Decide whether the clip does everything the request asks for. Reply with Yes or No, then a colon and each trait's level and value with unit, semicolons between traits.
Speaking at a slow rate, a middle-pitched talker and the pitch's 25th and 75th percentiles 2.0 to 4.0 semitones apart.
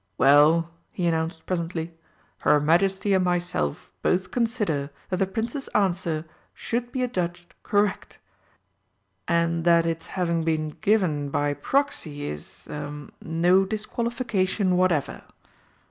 Yes: slow, 115 wpm; medium, 175 Hz; average, 3.6 semitones